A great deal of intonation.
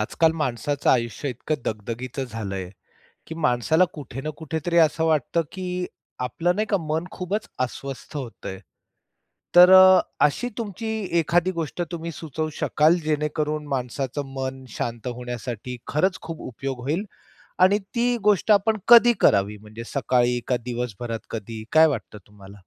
Yes: wide, 5.7 semitones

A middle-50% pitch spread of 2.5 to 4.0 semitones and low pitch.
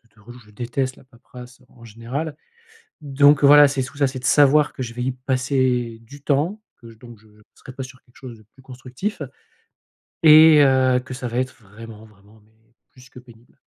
Yes: average, 2.8 semitones; low, 130 Hz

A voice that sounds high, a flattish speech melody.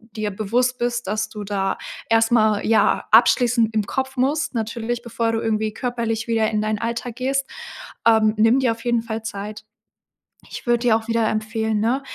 Yes: high, 225 Hz; narrow, 1.8 semitones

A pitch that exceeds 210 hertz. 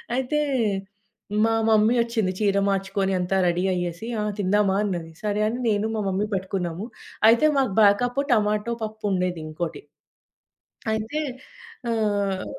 No: high, 205 Hz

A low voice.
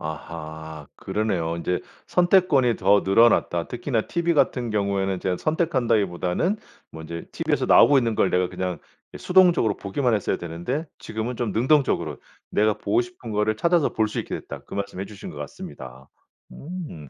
Yes: low, 105 Hz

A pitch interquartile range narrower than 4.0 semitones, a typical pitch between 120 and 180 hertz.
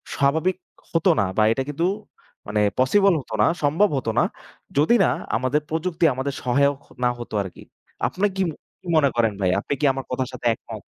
No: average, 5.1 semitones; medium, 140 Hz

